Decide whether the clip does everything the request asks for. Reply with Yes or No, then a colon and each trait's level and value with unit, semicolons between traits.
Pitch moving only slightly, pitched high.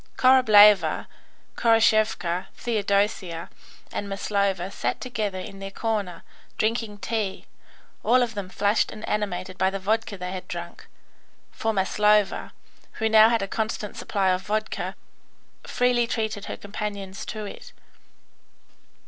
Yes: narrow, 2.3 semitones; high, 210 Hz